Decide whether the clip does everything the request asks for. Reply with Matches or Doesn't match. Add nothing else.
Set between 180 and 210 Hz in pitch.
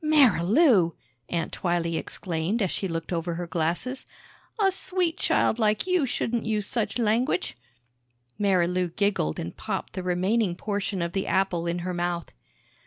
Matches